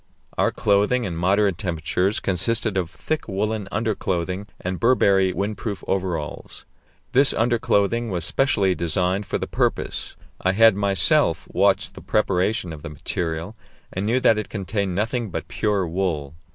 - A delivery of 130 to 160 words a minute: Yes, average, 145 wpm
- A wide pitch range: No, average, 3.1 semitones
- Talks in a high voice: No, very low, 95 Hz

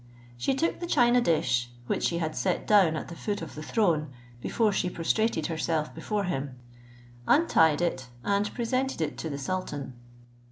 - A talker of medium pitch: Yes, medium, 170 Hz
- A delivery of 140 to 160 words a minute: No, average, 170 wpm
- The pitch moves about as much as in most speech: No, wide, 6.0 semitones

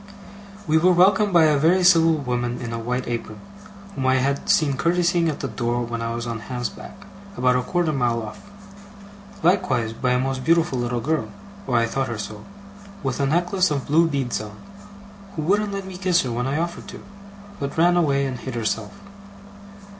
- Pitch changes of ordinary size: No, wide, 5.9 semitones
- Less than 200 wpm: No, fast, 205 wpm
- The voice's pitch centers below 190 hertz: Yes, low, 135 Hz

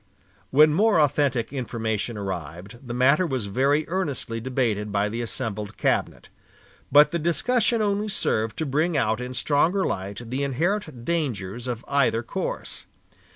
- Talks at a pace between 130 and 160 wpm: Yes, average, 145 wpm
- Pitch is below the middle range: Yes, low, 130 Hz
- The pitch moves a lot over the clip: Yes, wide, 5.7 semitones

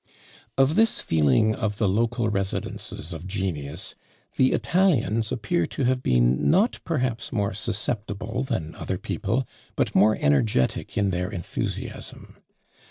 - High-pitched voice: No, low, 105 Hz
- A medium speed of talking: No, slow, 130 wpm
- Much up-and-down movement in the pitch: Yes, wide, 5.7 semitones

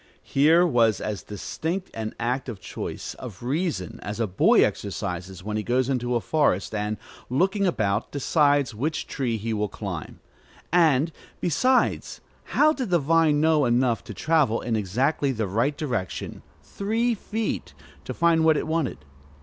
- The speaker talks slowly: No, average, 160 wpm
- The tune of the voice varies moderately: No, wide, 6.7 semitones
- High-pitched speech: No, low, 130 Hz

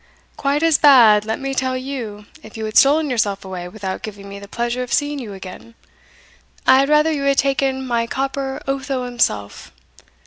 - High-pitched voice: Yes, very high, 250 Hz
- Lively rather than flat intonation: No, average, 4.5 semitones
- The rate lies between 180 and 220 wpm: Yes, average, 185 wpm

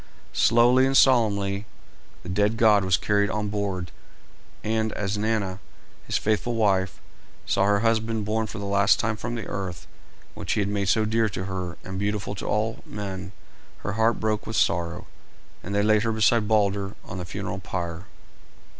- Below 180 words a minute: Yes, average, 170 wpm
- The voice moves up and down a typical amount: No, narrow, 2.1 semitones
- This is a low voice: Yes, low, 105 Hz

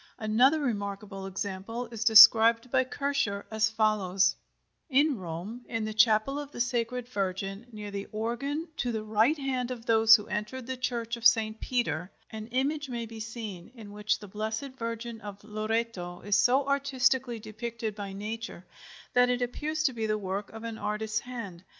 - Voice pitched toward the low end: No, high, 225 Hz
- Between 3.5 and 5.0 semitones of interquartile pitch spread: No, average, 3.0 semitones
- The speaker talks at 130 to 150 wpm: No, average, 175 wpm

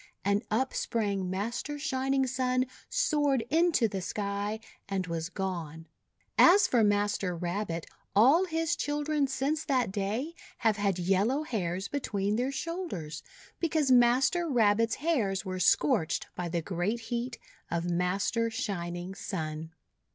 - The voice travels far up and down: Yes, wide, 6.3 semitones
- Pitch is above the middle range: Yes, high, 215 Hz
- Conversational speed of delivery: No, slow, 130 wpm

